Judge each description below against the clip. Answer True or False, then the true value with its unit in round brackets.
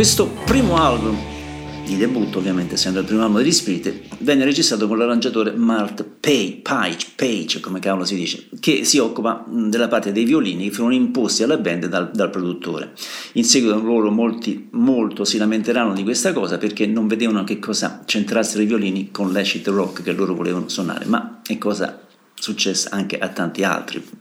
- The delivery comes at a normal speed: False (175 wpm)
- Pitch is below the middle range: True (105 Hz)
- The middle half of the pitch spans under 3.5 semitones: True (3.0 semitones)